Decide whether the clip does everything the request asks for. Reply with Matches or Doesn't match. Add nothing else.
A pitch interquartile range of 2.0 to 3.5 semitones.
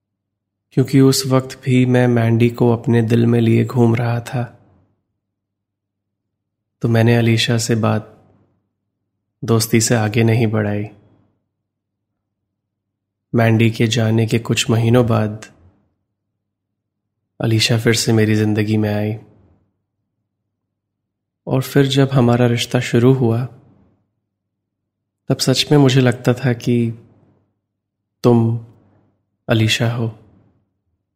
Matches